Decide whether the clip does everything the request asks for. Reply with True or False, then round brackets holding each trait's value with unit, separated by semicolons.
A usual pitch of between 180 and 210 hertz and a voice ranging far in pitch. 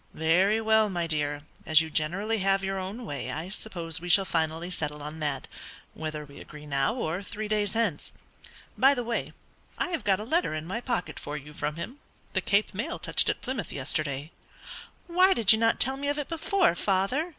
True (190 Hz; 6.4 semitones)